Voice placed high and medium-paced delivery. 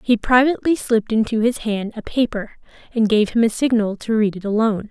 No: high, 225 Hz; fast, 210 wpm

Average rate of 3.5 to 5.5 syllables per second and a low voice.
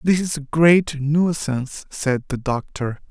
No: 3.9 syllables/s; medium, 150 Hz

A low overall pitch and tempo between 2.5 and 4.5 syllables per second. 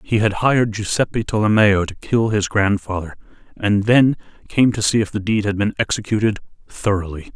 No: low, 105 Hz; 5.3 syllables/s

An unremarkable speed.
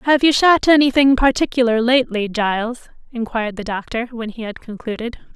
Yes: average, 155 wpm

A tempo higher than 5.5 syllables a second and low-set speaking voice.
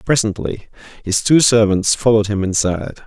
No: 5.4 syllables/s; low, 105 Hz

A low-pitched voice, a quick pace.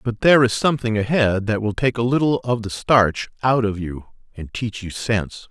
Yes: low, 115 Hz; fast, 220 wpm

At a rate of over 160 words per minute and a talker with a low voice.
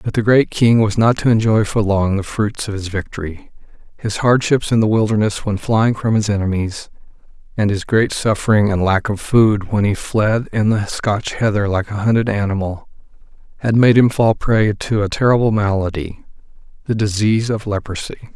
Yes: average, 185 wpm; low, 105 Hz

